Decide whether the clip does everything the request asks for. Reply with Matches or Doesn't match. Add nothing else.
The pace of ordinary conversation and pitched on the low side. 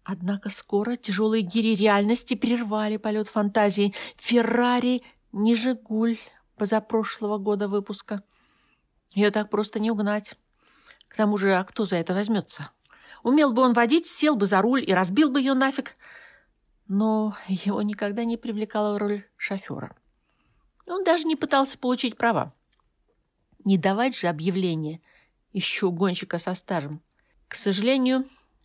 Doesn't match